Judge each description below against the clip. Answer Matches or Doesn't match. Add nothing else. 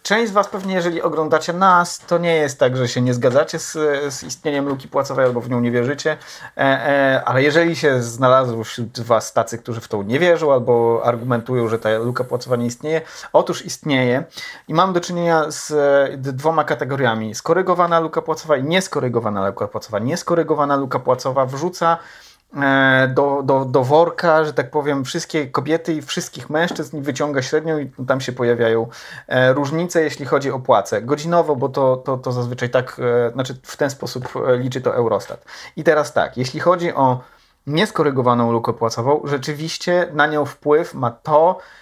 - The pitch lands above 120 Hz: Matches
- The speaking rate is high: Matches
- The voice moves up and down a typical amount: Matches